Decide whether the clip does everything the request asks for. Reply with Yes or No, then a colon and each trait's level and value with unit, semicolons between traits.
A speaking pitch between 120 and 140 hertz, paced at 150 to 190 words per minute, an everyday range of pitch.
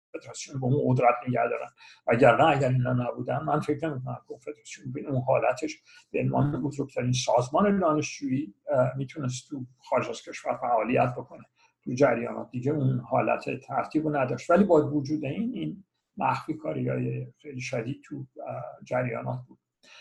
Yes: low, 135 Hz; fast, 155 wpm; average, 3.5 semitones